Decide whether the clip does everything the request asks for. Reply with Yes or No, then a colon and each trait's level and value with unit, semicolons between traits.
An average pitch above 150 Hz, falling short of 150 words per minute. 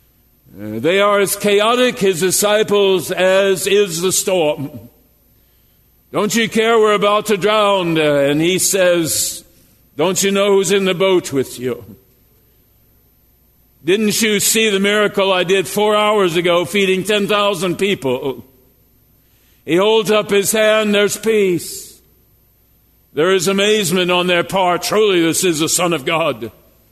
Yes: high, 190 Hz; average, 140 wpm